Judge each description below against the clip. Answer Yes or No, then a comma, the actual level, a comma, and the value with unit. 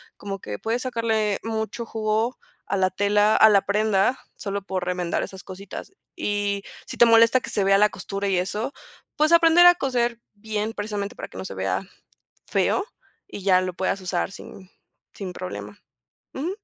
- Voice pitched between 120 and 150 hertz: No, high, 205 Hz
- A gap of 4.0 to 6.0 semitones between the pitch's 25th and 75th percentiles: No, average, 3.2 semitones